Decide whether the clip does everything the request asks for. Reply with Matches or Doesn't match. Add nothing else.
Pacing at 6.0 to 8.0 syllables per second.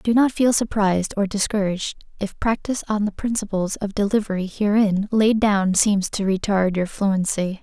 Doesn't match